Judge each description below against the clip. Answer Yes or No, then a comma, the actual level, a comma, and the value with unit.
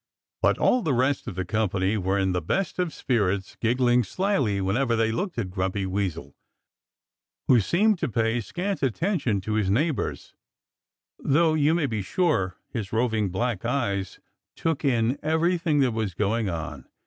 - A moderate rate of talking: Yes, average, 160 wpm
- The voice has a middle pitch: No, low, 115 Hz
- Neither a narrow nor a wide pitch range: No, wide, 7.0 semitones